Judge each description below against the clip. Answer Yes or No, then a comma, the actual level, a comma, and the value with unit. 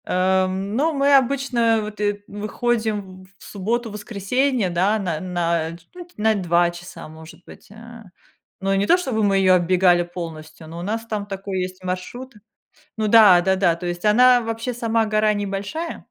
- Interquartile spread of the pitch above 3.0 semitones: Yes, average, 3.8 semitones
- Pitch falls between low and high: No, high, 205 Hz